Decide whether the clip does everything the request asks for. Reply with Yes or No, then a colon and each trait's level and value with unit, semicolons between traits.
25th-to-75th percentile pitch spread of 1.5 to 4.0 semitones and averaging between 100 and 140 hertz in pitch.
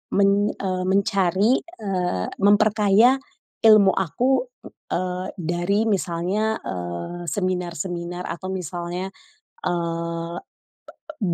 No: average, 2.7 semitones; medium, 185 Hz